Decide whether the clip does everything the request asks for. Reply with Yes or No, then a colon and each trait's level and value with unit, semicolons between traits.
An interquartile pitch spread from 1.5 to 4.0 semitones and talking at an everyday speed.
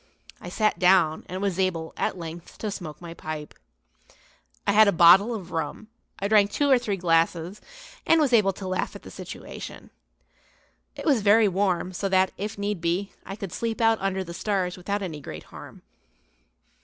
Yes: average, 3.2 semitones; average, 185 wpm